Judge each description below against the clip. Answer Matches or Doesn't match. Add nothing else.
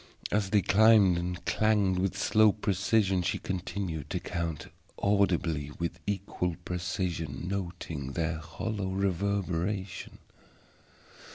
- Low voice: Matches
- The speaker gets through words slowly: Matches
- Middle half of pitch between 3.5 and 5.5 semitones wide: Doesn't match